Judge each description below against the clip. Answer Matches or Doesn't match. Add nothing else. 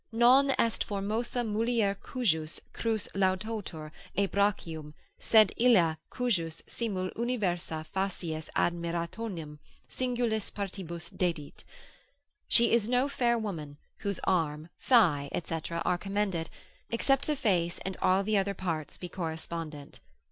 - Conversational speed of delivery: Doesn't match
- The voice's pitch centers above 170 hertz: Matches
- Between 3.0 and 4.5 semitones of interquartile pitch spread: Doesn't match